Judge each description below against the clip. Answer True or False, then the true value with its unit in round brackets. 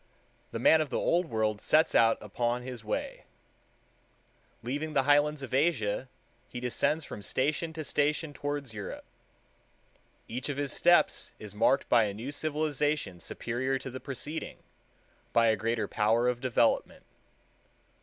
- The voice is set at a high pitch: False (130 Hz)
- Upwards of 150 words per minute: False (145 wpm)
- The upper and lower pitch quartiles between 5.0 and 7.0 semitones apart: False (4.4 semitones)